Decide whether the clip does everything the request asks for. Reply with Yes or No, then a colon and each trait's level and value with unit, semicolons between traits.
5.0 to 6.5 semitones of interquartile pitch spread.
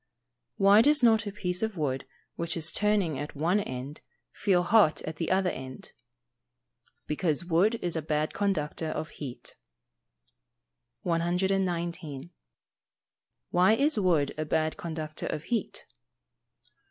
No: average, 4.2 semitones